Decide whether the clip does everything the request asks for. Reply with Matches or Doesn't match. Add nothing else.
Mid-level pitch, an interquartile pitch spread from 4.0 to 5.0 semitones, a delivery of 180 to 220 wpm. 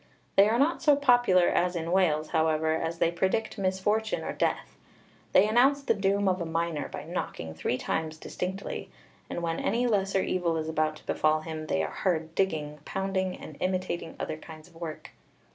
Doesn't match